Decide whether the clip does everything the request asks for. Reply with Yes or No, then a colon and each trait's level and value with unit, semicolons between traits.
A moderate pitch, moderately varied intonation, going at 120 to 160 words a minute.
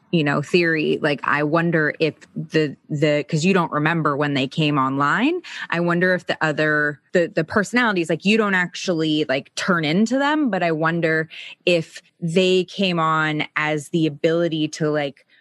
No: medium, 160 Hz; average, 3.0 semitones; average, 175 wpm